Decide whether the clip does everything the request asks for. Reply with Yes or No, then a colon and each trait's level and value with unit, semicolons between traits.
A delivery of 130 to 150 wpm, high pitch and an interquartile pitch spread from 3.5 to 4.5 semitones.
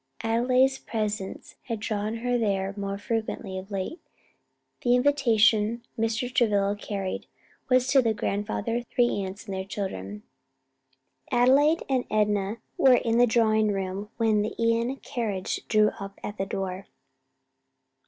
No: average, 140 wpm; high, 220 Hz; average, 3.1 semitones